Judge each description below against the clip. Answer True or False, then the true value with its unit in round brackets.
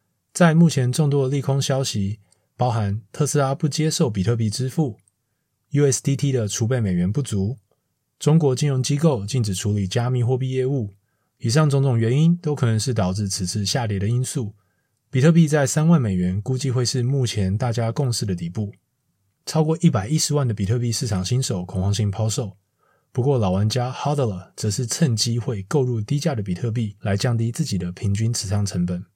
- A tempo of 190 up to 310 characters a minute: True (300 characters per minute)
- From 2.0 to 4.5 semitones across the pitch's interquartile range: False (5.0 semitones)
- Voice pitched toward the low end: True (120 Hz)